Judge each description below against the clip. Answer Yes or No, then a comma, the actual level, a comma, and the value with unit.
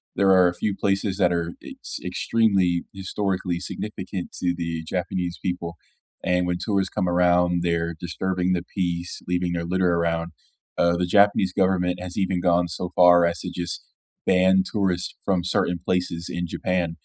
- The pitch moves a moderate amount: No, narrow, 1.3 semitones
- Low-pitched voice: Yes, very low, 90 Hz